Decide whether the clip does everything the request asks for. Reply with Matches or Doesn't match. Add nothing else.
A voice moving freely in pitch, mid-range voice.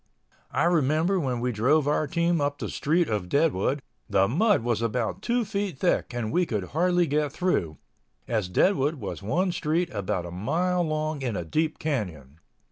Matches